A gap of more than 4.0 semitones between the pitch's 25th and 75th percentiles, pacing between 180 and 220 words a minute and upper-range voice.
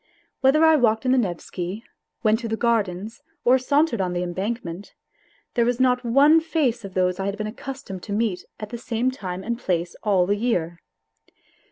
Yes: average, 4.9 semitones; average, 190 wpm; high, 220 Hz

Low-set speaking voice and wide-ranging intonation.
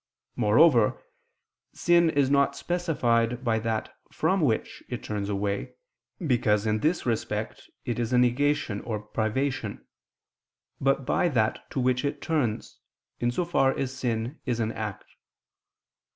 No: low, 125 Hz; average, 4.3 semitones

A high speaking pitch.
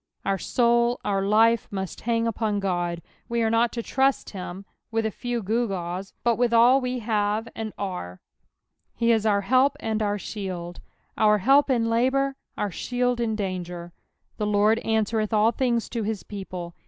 Yes: high, 220 Hz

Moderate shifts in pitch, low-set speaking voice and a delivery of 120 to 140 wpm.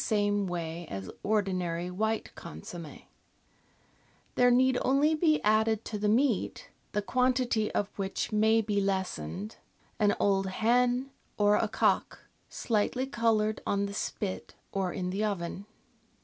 No: average, 3.1 semitones; high, 210 Hz; slow, 135 wpm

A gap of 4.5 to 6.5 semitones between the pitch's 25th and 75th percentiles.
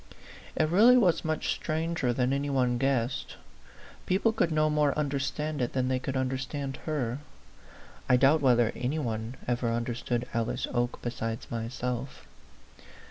No: average, 3.9 semitones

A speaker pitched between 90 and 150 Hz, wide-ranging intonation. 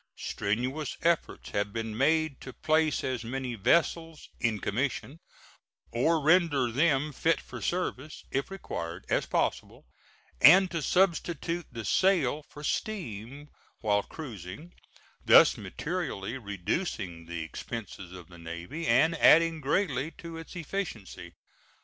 Yes: medium, 140 Hz; wide, 7.0 semitones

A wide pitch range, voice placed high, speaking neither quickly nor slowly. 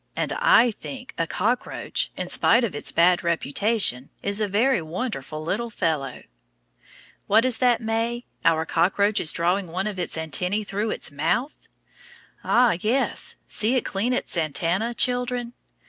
Yes: wide, 6.0 semitones; high, 205 Hz; average, 150 wpm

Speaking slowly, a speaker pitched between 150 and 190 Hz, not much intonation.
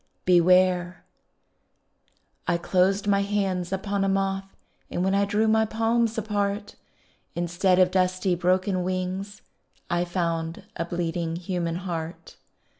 Yes: slow, 120 wpm; medium, 185 Hz; narrow, 2.2 semitones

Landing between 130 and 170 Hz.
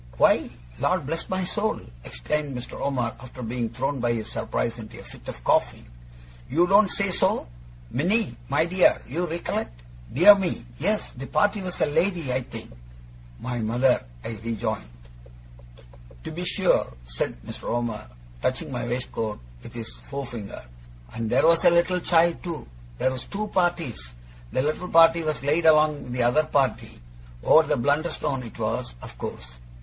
Yes: medium, 140 Hz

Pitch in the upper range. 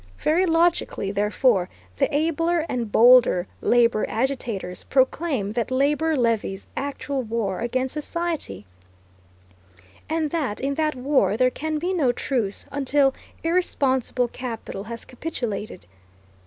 Yes: very high, 260 Hz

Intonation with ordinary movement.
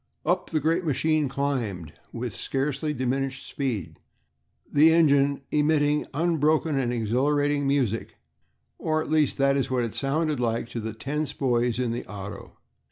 Yes: average, 3.7 semitones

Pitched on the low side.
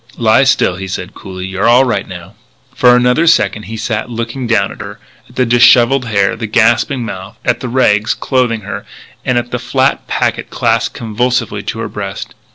Yes: low, 115 Hz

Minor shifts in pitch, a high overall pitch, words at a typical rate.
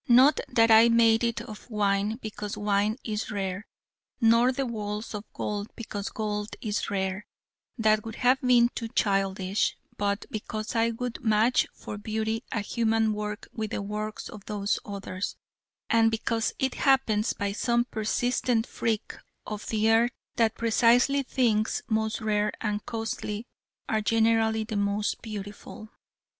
Yes: narrow, 1.7 semitones; high, 220 Hz; average, 150 wpm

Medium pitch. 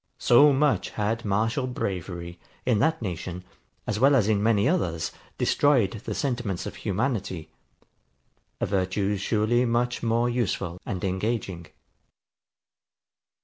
No: low, 105 Hz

